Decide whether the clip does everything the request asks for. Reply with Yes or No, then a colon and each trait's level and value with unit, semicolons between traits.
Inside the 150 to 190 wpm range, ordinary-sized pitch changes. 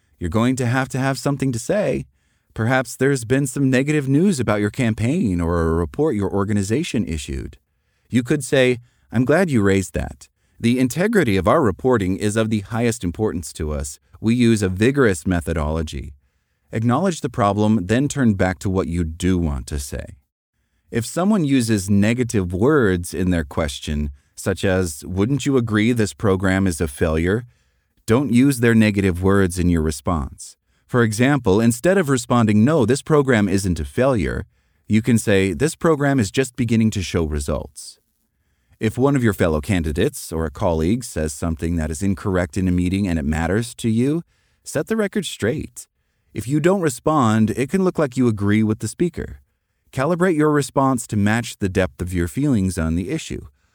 No: average, 180 wpm; wide, 6.5 semitones